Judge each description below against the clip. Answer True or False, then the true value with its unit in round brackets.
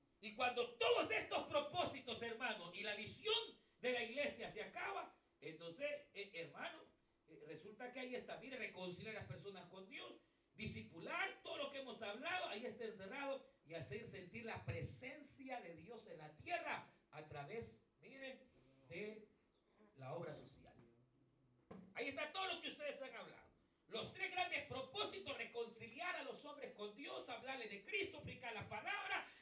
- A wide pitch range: True (6.4 semitones)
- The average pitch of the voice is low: False (240 Hz)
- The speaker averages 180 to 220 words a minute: False (160 wpm)